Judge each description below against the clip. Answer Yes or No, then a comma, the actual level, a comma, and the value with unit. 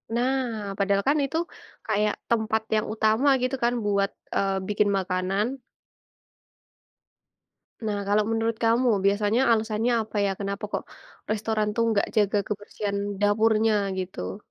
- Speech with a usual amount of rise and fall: No, narrow, 2.0 semitones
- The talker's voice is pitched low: No, high, 215 Hz